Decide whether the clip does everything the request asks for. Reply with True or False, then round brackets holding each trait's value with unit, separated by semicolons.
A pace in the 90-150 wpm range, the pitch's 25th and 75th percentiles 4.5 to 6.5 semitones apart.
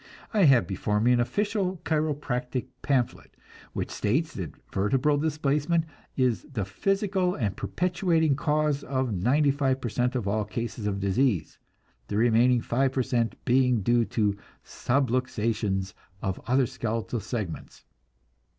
True (135 wpm; 4.8 semitones)